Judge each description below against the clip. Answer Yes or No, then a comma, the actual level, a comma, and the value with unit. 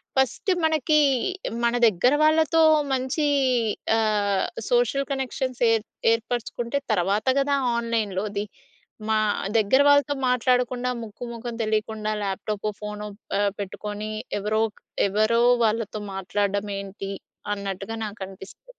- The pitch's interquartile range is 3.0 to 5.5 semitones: Yes, average, 3.6 semitones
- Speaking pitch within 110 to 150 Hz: No, high, 220 Hz